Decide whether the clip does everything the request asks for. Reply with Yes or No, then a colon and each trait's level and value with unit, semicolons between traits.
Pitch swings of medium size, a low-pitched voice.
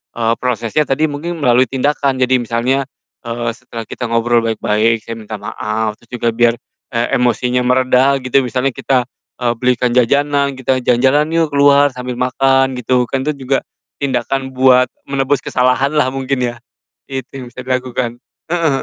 No: narrow, 2.3 semitones; low, 125 Hz